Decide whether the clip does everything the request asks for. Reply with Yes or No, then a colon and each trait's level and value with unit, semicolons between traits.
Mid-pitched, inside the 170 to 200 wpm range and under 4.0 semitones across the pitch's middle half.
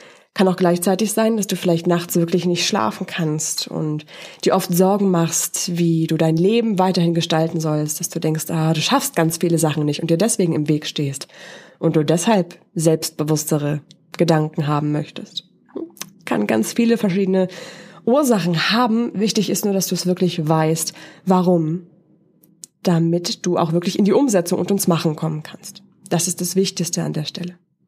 Yes: medium, 175 Hz; average, 175 wpm; average, 2.8 semitones